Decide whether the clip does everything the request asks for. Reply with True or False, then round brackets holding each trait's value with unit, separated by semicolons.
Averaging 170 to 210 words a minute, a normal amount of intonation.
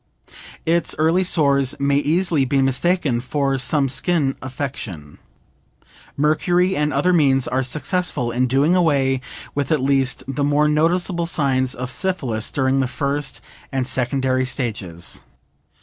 False (135 wpm; 3.1 semitones)